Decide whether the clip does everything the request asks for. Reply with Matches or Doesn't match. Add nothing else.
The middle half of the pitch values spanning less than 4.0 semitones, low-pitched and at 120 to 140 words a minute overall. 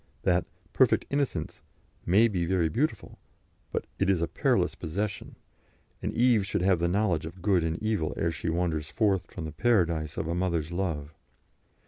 Doesn't match